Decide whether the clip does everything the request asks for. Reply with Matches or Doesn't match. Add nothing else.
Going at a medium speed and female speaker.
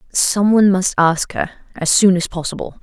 Matches